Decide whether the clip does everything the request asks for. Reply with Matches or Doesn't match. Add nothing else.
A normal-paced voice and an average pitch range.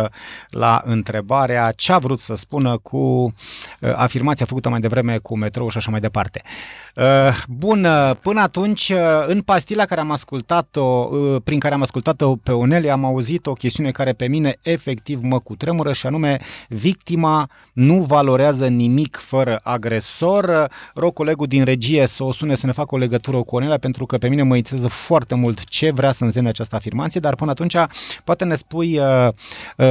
Doesn't match